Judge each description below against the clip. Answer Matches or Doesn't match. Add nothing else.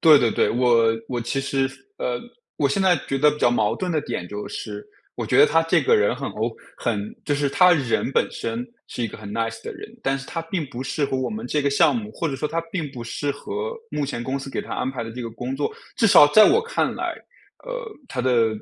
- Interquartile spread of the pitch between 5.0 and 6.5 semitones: Matches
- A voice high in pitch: Doesn't match